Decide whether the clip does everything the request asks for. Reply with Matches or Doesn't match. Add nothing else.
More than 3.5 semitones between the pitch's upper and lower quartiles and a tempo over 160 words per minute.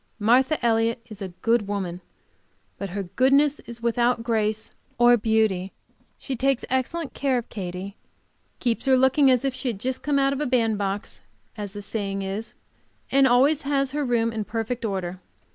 Matches